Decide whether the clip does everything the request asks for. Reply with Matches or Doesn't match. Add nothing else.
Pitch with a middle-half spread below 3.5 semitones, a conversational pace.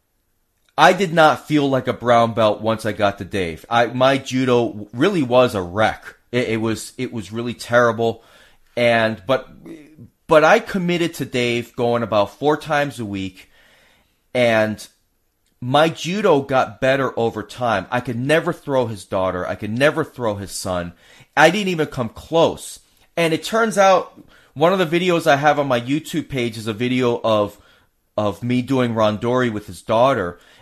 Doesn't match